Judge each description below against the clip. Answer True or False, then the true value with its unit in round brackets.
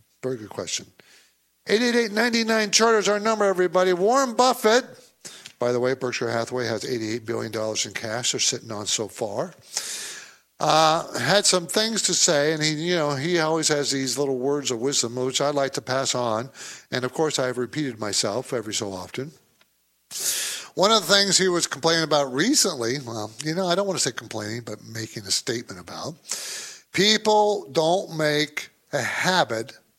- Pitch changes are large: True (7.8 semitones)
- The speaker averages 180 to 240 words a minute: True (185 wpm)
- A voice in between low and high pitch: True (145 Hz)